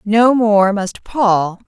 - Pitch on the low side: No, high, 210 Hz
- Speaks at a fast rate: No, average, 145 wpm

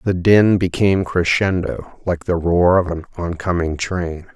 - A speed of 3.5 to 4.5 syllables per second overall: Yes, 4.4 syllables/s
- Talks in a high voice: No, very low, 90 Hz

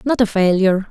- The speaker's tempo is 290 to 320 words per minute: No, average, 200 wpm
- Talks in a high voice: Yes, high, 205 Hz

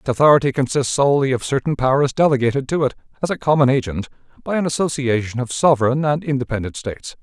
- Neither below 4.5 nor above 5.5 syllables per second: No, 6.7 syllables/s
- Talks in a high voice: No, low, 135 Hz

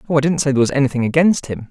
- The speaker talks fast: Yes, fast, 315 wpm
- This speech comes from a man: Yes, male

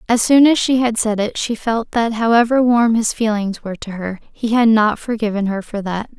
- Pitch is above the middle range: Yes, high, 225 Hz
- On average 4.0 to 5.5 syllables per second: Yes, 5.1 syllables/s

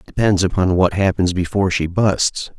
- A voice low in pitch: Yes, very low, 95 Hz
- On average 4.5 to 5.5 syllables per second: Yes, 5.0 syllables/s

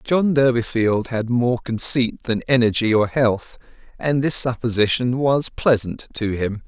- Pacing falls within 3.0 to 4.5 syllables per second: Yes, 4.1 syllables/s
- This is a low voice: Yes, low, 120 Hz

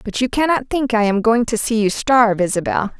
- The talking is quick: Yes, fast, 240 wpm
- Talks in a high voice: Yes, high, 230 Hz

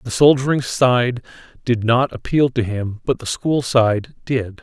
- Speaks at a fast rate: No, average, 170 wpm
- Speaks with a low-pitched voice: Yes, low, 125 Hz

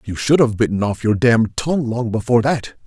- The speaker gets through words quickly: Yes, fast, 210 wpm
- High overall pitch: No, low, 115 Hz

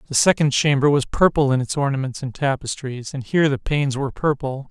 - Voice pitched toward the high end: No, medium, 140 Hz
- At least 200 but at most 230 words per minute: Yes, fast, 205 wpm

